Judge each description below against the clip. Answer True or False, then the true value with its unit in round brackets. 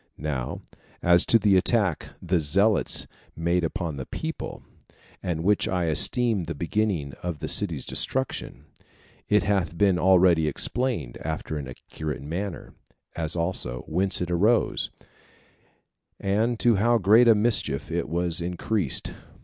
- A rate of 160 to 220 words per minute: False (135 wpm)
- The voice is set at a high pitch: False (90 Hz)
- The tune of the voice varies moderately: True (4.6 semitones)